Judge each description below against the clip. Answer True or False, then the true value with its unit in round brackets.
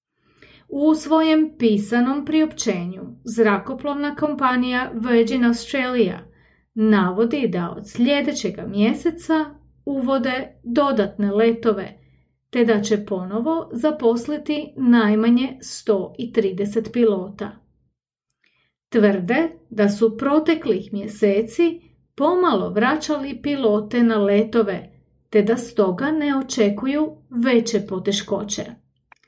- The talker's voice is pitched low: False (235 Hz)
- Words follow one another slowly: True (85 wpm)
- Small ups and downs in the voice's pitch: False (5.1 semitones)